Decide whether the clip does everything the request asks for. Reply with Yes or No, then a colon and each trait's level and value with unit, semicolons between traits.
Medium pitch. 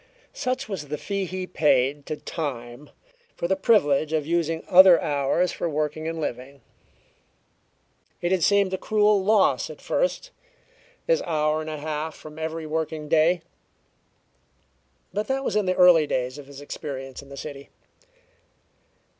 Yes: medium, 160 Hz